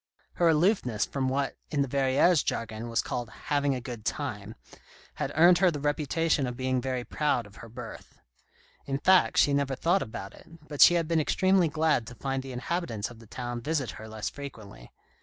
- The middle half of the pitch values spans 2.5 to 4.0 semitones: No, average, 4.6 semitones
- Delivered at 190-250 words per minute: Yes, average, 200 wpm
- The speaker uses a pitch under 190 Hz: Yes, low, 135 Hz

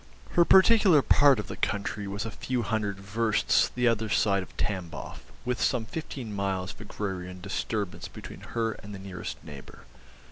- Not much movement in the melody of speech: No, average, 3.2 semitones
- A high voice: No, low, 105 Hz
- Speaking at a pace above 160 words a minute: Yes, average, 170 wpm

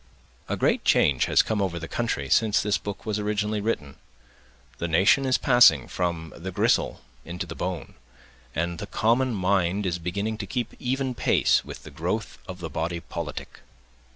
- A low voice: Yes, very low, 95 Hz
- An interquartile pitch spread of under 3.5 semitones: No, average, 4.2 semitones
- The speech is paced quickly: No, average, 175 wpm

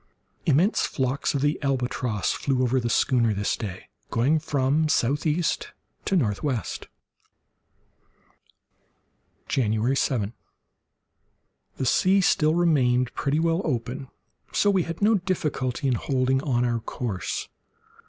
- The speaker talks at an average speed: No, slow, 115 wpm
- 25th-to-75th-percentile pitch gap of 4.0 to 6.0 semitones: Yes, average, 4.3 semitones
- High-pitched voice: No, low, 135 Hz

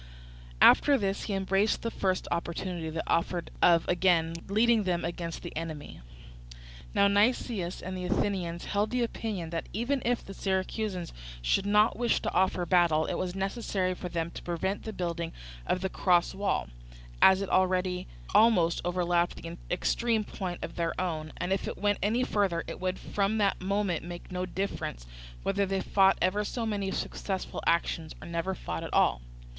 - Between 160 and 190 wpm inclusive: Yes, average, 175 wpm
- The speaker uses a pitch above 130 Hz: Yes, medium, 185 Hz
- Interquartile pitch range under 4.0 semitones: Yes, average, 2.8 semitones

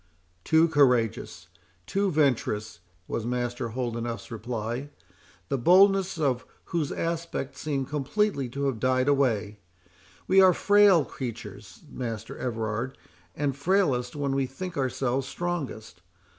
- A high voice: No, low, 130 Hz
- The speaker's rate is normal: No, slow, 115 wpm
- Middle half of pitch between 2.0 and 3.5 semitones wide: No, average, 5.2 semitones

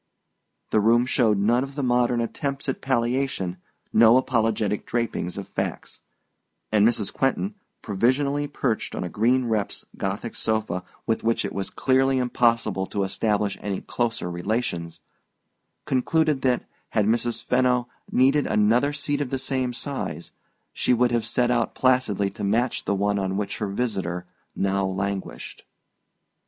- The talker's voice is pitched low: Yes, low, 115 Hz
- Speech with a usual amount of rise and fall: Yes, average, 4.0 semitones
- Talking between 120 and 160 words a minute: Yes, average, 145 wpm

